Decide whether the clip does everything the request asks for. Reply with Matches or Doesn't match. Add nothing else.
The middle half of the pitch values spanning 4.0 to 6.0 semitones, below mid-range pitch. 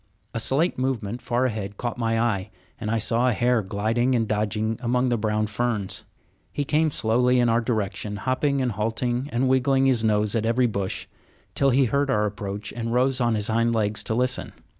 Doesn't match